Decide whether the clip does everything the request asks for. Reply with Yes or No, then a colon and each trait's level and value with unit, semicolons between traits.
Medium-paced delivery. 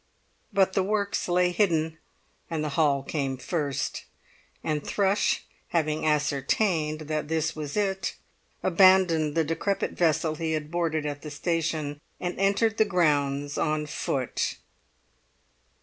No: slow, 130 wpm